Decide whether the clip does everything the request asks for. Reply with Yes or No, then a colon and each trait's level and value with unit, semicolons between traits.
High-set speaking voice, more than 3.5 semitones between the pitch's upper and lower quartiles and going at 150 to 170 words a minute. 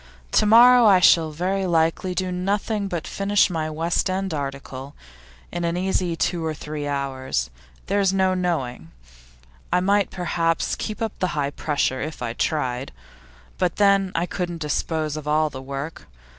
No: medium, 170 Hz; average, 4.2 semitones; average, 160 wpm